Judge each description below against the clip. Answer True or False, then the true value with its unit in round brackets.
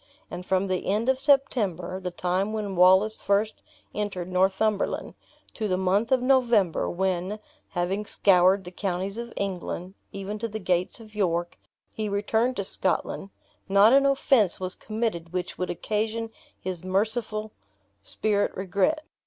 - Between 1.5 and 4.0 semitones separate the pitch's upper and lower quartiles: True (2.9 semitones)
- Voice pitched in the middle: False (200 Hz)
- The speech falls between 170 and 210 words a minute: False (145 wpm)